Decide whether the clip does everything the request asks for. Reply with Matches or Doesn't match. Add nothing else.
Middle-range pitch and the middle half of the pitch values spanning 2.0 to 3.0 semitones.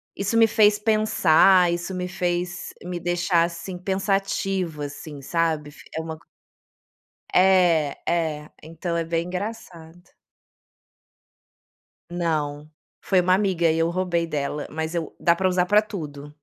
Matches